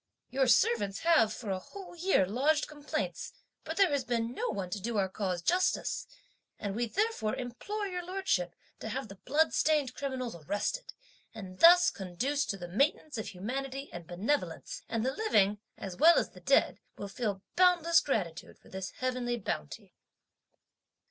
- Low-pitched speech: No, high, 240 Hz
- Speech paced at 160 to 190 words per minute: Yes, average, 165 wpm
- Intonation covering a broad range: Yes, wide, 7.7 semitones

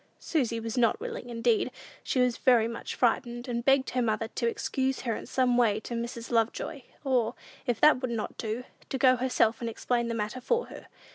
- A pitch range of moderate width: No, narrow, 1.8 semitones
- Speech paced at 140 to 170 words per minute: No, fast, 205 wpm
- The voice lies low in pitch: No, high, 240 Hz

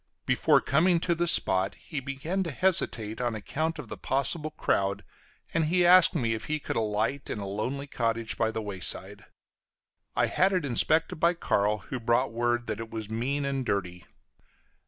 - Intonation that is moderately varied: No, wide, 6.2 semitones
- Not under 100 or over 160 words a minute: No, average, 180 wpm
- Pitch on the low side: Yes, low, 125 Hz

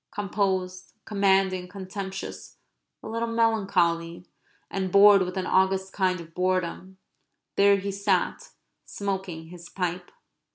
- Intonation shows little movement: Yes, narrow, 1.5 semitones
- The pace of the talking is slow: Yes, slow, 115 wpm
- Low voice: No, high, 190 Hz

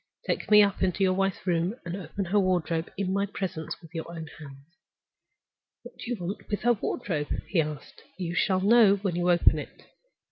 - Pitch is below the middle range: No, medium, 185 Hz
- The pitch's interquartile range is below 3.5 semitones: Yes, average, 2.9 semitones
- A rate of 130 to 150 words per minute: No, average, 200 wpm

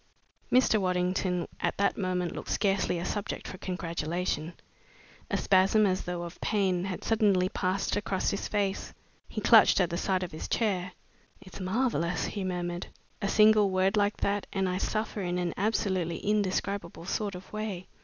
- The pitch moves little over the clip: Yes, narrow, 2.2 semitones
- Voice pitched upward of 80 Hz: Yes, high, 190 Hz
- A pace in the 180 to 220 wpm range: No, average, 165 wpm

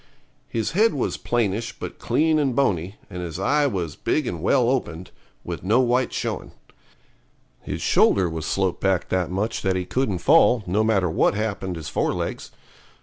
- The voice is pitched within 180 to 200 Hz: No, low, 100 Hz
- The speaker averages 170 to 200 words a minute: Yes, average, 175 wpm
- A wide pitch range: Yes, wide, 5.8 semitones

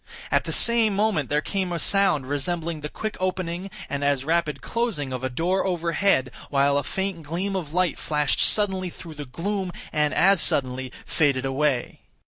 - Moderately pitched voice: Yes, medium, 165 Hz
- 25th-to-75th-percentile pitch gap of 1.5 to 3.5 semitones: No, average, 5.0 semitones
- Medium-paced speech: Yes, average, 175 wpm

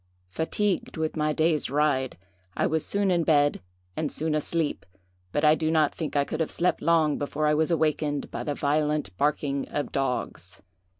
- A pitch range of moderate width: No, narrow, 1.7 semitones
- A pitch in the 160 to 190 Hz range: No, medium, 150 Hz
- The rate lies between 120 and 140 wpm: No, average, 180 wpm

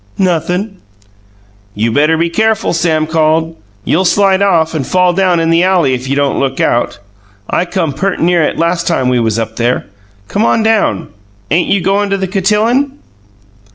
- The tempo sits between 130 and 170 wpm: No, average, 180 wpm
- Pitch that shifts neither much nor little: Yes, average, 4.1 semitones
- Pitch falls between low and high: Yes, medium, 170 Hz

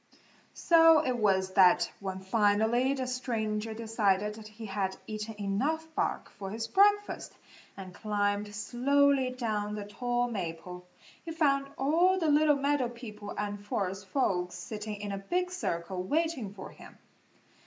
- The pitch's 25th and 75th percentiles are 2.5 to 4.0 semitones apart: No, wide, 5.4 semitones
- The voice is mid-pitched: No, high, 215 Hz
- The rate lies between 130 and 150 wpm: Yes, average, 145 wpm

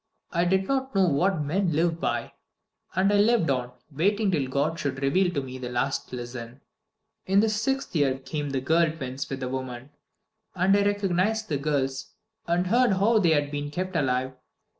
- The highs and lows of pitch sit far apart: Yes, wide, 6.3 semitones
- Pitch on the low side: No, medium, 160 Hz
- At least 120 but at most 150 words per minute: No, average, 185 wpm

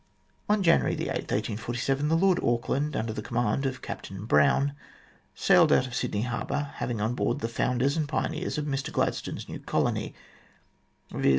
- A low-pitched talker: Yes, low, 130 Hz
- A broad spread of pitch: No, average, 3.9 semitones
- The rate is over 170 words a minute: No, average, 165 wpm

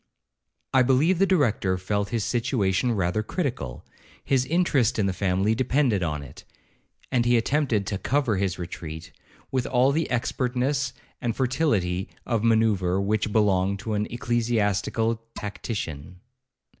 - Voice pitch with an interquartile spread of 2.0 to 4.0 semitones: No, average, 4.7 semitones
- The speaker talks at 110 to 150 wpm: Yes, slow, 135 wpm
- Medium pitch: No, low, 110 Hz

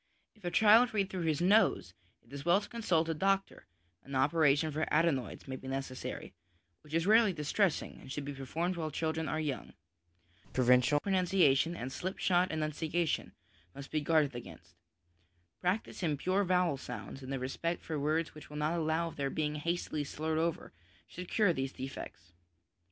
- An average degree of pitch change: Yes, average, 4.0 semitones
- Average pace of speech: Yes, average, 175 wpm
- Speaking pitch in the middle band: Yes, medium, 160 Hz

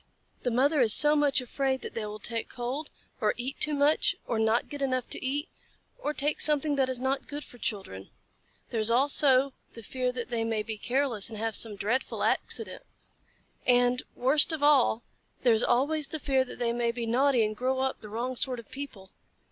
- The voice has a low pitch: No, very high, 255 Hz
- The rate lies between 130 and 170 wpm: No, fast, 205 wpm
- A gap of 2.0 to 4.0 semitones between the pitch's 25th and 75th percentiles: Yes, average, 3.4 semitones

